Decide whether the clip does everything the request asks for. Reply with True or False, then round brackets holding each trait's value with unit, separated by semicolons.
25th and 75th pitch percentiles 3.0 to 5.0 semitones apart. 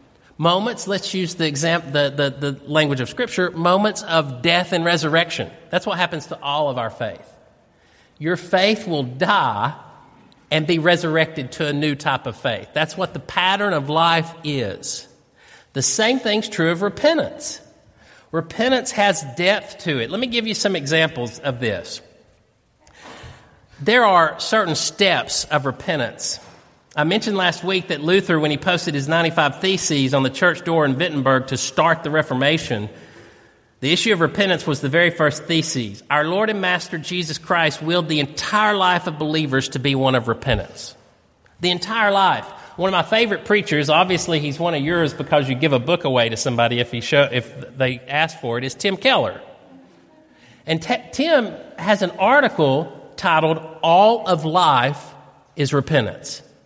True (4.6 semitones)